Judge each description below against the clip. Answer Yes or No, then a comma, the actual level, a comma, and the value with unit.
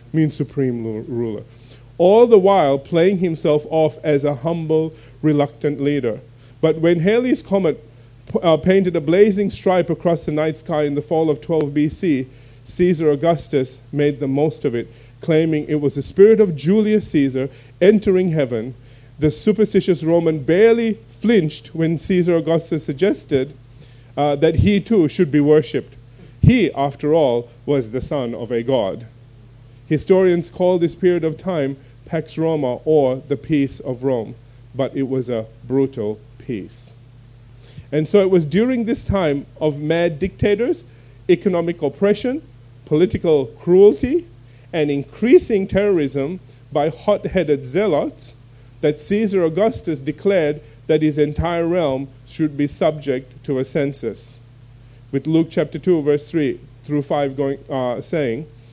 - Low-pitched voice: No, medium, 150 Hz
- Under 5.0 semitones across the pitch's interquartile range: No, wide, 5.4 semitones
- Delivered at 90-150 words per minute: Yes, average, 140 wpm